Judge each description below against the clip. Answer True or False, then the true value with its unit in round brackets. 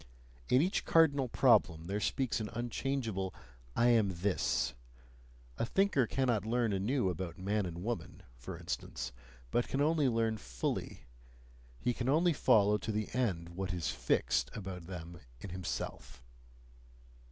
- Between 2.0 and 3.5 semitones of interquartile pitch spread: False (5.4 semitones)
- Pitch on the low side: True (105 Hz)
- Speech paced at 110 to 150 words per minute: True (140 wpm)